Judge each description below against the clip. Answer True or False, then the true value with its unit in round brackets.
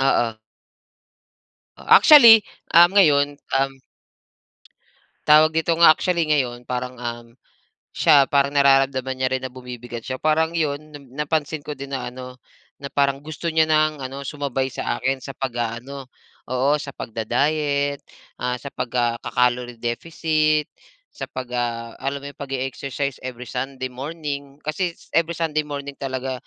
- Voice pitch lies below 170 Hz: True (140 Hz)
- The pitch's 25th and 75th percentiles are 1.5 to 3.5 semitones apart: True (3.2 semitones)